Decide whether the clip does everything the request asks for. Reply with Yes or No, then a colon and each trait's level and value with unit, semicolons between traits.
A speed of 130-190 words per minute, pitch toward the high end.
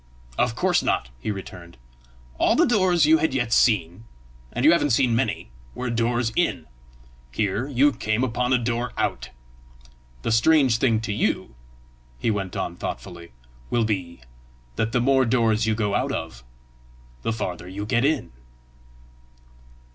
No: average, 155 wpm; low, 115 Hz